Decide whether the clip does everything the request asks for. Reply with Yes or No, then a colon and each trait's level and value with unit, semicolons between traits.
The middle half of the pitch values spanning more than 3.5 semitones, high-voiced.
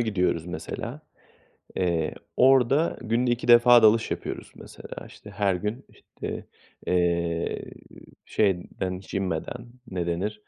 No: average, 5.1 semitones; low, 100 Hz